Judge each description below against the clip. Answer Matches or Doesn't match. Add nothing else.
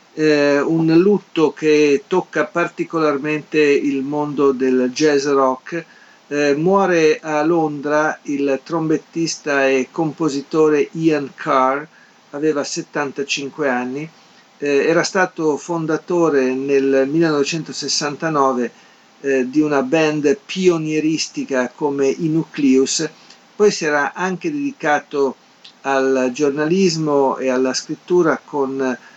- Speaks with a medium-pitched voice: Matches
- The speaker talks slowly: Matches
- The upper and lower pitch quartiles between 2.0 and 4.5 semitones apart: Matches